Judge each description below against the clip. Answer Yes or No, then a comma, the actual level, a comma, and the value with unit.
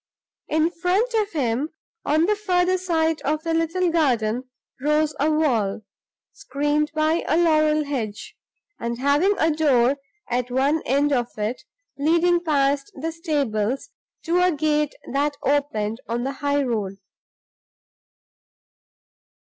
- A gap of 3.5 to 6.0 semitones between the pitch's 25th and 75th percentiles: Yes, average, 3.9 semitones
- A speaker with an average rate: No, slow, 130 wpm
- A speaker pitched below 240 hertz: No, very high, 295 Hz